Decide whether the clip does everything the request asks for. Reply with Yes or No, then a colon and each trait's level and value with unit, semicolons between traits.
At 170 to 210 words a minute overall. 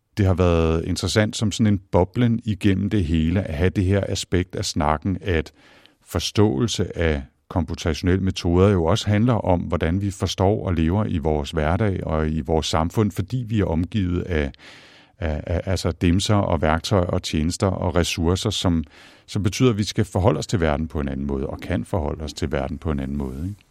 Yes: average, 200 wpm